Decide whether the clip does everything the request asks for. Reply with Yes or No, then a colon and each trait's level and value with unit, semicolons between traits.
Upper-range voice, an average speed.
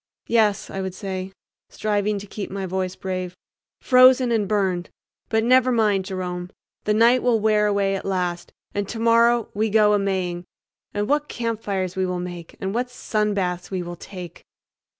Yes: high, 200 Hz; average, 170 wpm